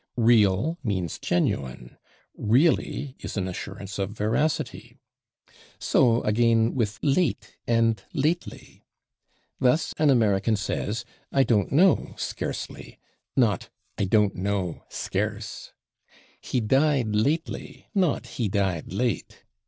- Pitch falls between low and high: No, low, 110 Hz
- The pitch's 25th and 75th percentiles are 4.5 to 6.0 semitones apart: Yes, average, 4.8 semitones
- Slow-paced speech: Yes, slow, 105 wpm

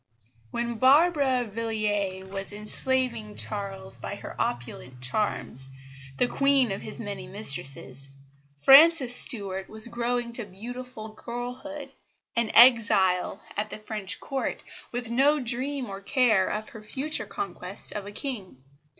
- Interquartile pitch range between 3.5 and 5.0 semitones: Yes, average, 4.2 semitones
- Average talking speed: No, slow, 130 wpm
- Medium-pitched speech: No, high, 225 Hz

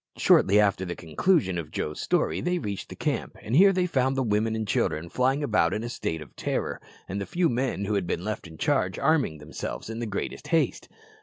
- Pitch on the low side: Yes, low, 105 Hz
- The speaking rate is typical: No, fast, 225 wpm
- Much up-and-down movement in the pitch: Yes, wide, 6.7 semitones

